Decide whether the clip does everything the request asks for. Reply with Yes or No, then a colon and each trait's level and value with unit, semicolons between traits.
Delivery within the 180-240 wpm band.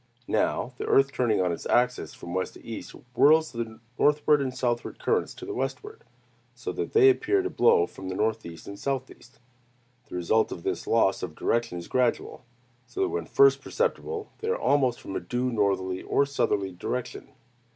Yes: average, 185 wpm